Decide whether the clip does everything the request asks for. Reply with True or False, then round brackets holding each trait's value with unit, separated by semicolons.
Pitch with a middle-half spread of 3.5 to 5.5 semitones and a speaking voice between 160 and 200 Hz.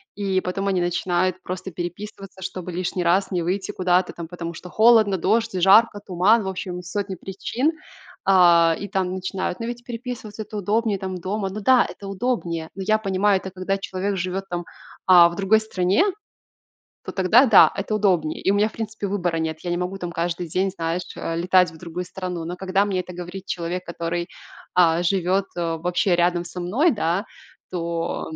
False (2.4 semitones; 185 Hz)